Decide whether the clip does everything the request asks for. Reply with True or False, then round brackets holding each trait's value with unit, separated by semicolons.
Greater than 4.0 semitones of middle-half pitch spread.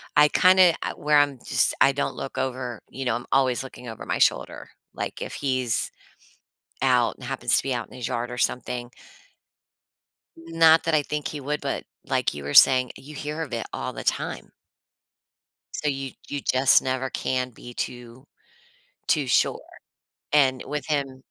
False (2.9 semitones)